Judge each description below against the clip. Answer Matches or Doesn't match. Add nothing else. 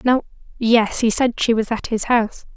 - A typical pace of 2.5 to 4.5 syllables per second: Doesn't match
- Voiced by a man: Doesn't match